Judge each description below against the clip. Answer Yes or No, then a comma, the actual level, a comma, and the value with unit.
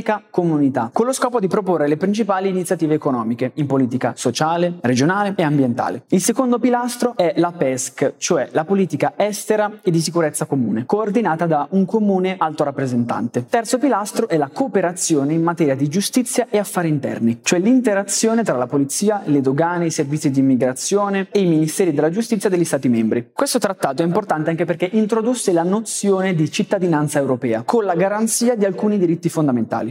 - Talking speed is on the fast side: Yes, fast, 175 wpm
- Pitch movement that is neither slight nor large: No, wide, 6.2 semitones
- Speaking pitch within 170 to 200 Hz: Yes, medium, 175 Hz